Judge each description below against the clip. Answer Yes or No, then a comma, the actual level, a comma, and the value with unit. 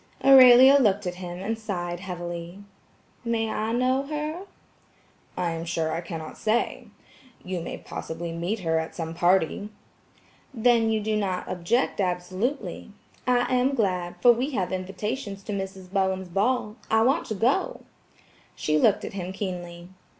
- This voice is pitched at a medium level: No, high, 195 Hz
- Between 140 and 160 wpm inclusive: Yes, average, 150 wpm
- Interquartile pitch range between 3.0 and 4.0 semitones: No, average, 4.9 semitones